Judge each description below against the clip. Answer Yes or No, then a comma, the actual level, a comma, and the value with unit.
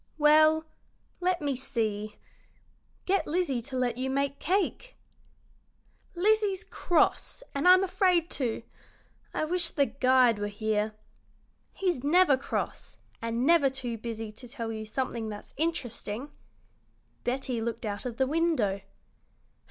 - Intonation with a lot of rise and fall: Yes, wide, 6.5 semitones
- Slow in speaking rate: Yes, slow, 130 wpm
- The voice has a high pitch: Yes, very high, 265 Hz